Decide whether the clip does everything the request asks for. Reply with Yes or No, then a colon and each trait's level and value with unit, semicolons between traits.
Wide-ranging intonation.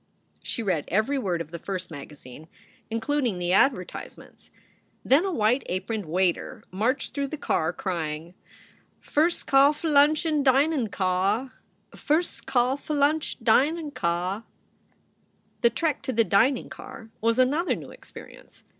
Yes: wide, 7.6 semitones